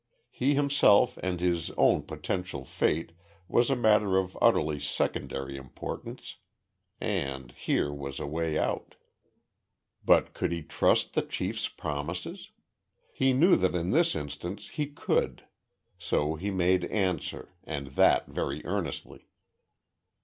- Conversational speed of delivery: No, slow, 125 wpm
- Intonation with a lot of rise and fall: Yes, wide, 6.1 semitones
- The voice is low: Yes, very low, 90 Hz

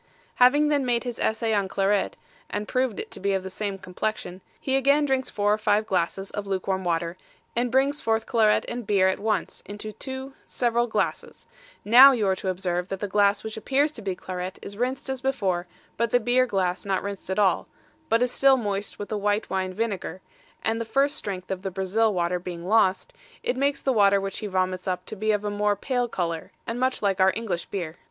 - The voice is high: Yes, high, 205 Hz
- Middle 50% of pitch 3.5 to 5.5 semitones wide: Yes, average, 4.2 semitones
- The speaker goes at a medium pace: No, fast, 220 wpm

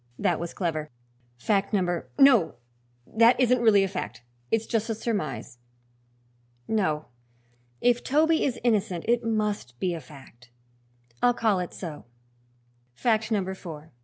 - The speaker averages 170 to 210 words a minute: No, slow, 135 wpm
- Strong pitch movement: Yes, wide, 5.8 semitones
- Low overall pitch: No, high, 200 Hz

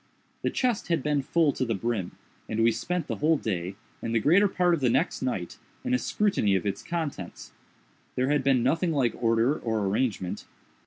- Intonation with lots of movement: Yes, wide, 6.3 semitones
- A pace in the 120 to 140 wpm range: No, average, 200 wpm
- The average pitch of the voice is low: Yes, low, 130 Hz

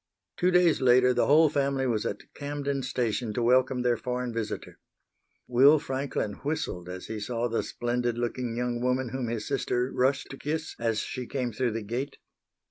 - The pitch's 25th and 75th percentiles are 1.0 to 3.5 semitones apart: Yes, narrow, 2.5 semitones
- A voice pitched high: No, low, 125 Hz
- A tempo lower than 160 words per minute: No, average, 180 wpm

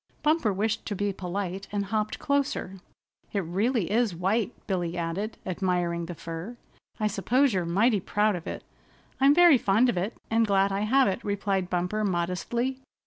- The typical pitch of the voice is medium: No, high, 200 Hz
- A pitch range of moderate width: Yes, average, 3.9 semitones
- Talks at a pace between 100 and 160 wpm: No, average, 170 wpm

